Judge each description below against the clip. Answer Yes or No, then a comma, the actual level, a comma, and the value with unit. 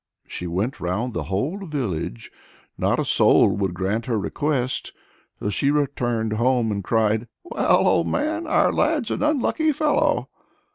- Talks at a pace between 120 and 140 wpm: No, average, 150 wpm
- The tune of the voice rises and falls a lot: Yes, wide, 7.3 semitones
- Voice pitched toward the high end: No, low, 120 Hz